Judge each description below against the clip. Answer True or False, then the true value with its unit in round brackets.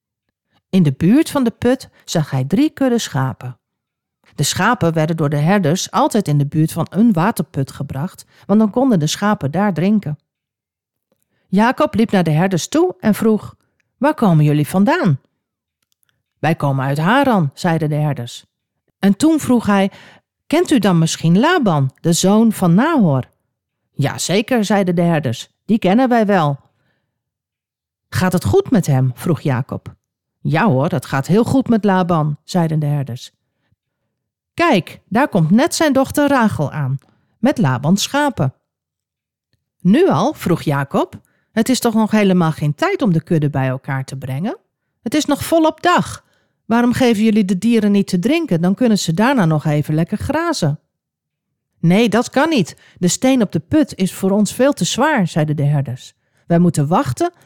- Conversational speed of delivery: True (170 wpm)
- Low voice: False (185 Hz)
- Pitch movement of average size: False (7.7 semitones)